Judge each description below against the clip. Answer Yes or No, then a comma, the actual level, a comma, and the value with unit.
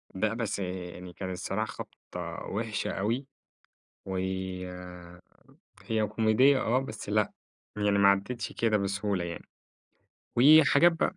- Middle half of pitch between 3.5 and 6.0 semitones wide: No, average, 3.1 semitones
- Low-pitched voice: Yes, low, 105 Hz